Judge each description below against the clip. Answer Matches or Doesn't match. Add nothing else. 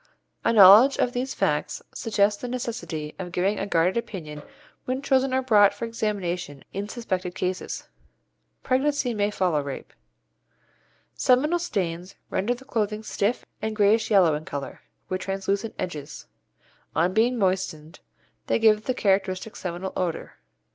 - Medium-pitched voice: Doesn't match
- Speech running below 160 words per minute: Matches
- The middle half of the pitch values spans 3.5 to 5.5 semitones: Matches